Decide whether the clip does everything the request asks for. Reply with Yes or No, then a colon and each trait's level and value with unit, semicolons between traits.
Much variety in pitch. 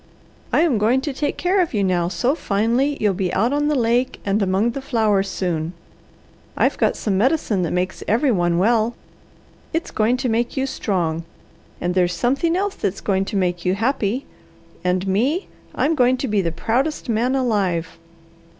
Yes: wide, 5.9 semitones